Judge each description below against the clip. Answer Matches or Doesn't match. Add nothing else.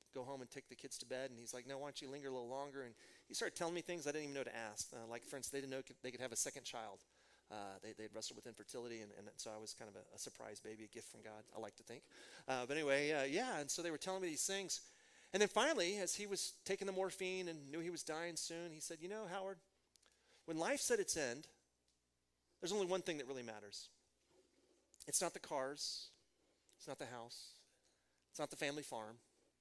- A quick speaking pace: Matches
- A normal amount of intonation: Doesn't match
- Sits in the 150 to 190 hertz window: Doesn't match